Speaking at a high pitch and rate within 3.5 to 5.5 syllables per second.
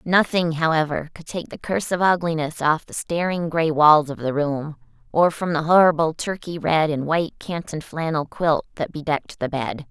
No: medium, 160 Hz; 5.0 syllables/s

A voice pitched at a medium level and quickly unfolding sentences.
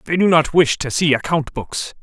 Yes: medium, 155 Hz; fast, 235 wpm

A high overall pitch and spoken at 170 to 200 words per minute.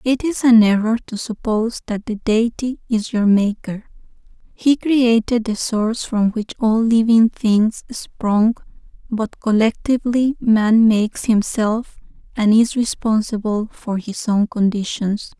No: high, 220 Hz; slow, 135 wpm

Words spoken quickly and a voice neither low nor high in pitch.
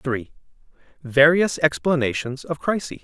No: slow, 100 wpm; medium, 150 Hz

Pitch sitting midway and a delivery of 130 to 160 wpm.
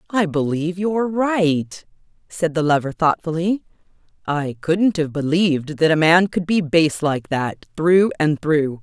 Yes: medium, 165 Hz; average, 155 wpm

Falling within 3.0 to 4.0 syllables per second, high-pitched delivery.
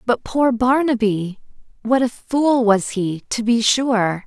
Yes: 3.5 syllables/s; high, 235 Hz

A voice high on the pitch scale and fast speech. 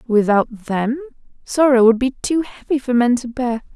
No: very high, 250 Hz; average, 175 wpm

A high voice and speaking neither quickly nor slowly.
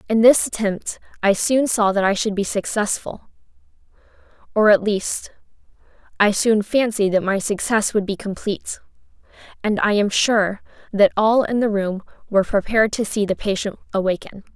Yes: high, 210 Hz; average, 150 wpm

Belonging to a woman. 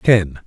No: male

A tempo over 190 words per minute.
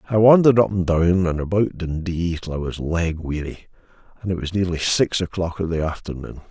Yes: fast, 205 wpm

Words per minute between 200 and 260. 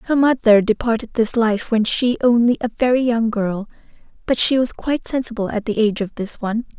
Yes: fast, 205 wpm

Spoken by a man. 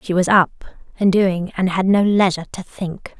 No: female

